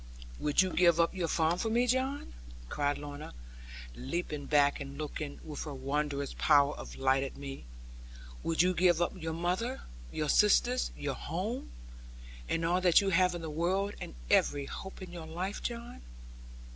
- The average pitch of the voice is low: No, medium, 165 Hz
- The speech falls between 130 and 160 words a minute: No, average, 170 wpm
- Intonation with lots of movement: No, average, 4.2 semitones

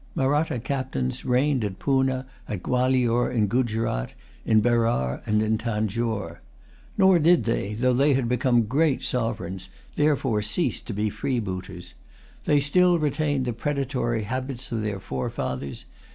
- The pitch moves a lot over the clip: No, average, 4.1 semitones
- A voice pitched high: No, low, 120 Hz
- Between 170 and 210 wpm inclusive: No, average, 140 wpm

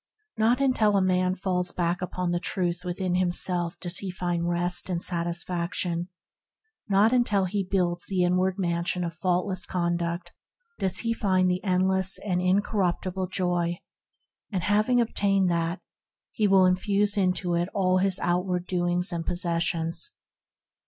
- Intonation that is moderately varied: No, narrow, 1.7 semitones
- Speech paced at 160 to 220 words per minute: No, average, 145 wpm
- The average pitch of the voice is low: No, medium, 180 Hz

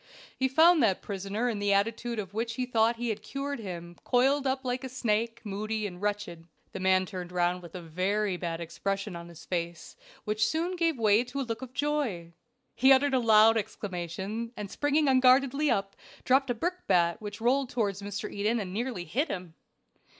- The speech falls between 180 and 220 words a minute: Yes, average, 195 wpm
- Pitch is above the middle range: Yes, high, 215 Hz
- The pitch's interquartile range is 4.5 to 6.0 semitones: Yes, average, 5.3 semitones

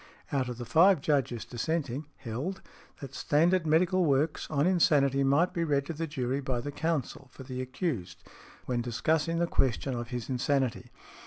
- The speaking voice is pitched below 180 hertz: Yes, medium, 140 Hz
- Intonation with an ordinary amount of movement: Yes, average, 4.2 semitones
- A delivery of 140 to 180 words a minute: Yes, average, 175 wpm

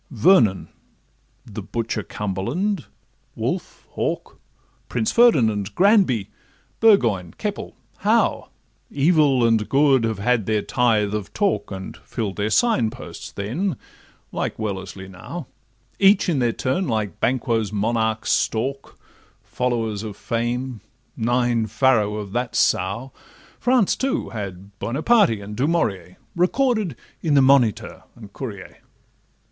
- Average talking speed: No, slow, 120 wpm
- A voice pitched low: Yes, low, 115 Hz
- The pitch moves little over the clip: No, average, 5.2 semitones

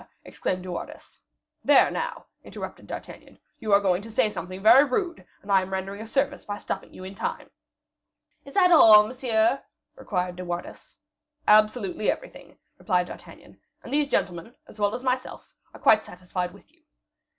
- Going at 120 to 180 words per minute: Yes, average, 170 wpm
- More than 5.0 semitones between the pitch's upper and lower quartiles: Yes, wide, 5.4 semitones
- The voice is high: Yes, high, 210 Hz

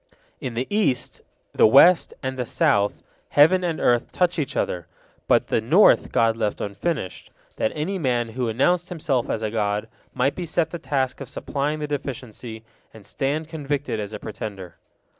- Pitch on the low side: Yes, low, 130 Hz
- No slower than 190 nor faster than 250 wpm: No, average, 175 wpm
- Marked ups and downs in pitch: Yes, wide, 5.8 semitones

